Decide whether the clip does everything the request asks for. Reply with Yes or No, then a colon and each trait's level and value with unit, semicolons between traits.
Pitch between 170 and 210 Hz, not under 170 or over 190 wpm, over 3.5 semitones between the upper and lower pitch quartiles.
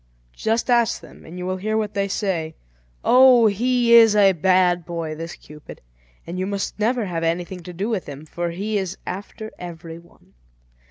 Yes: medium, 185 Hz; average, 185 wpm; average, 4.2 semitones